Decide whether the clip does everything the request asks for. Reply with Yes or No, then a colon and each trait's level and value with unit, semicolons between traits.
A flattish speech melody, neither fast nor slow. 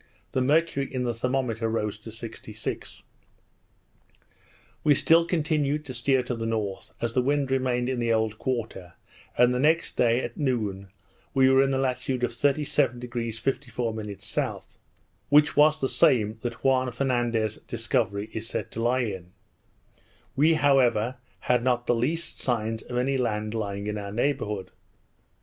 No: average, 3.2 semitones; average, 155 wpm